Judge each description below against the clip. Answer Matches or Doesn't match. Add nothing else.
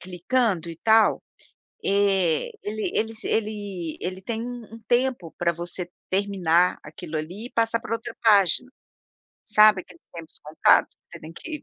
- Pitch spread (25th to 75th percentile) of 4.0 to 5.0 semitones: Matches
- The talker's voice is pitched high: Matches